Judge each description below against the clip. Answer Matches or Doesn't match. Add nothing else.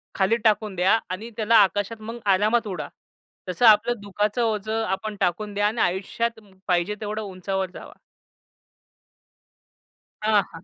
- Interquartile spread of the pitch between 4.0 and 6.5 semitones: Doesn't match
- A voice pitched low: Doesn't match